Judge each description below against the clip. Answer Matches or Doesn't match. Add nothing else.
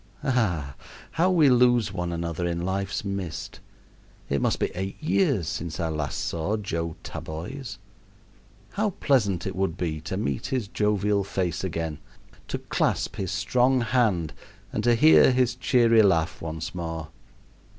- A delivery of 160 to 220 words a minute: Doesn't match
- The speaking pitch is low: Matches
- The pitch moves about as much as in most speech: Doesn't match